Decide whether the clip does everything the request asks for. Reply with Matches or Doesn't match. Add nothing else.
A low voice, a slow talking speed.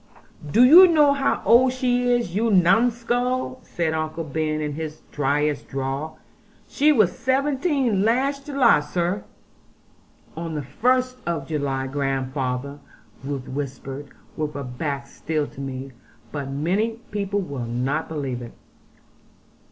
Doesn't match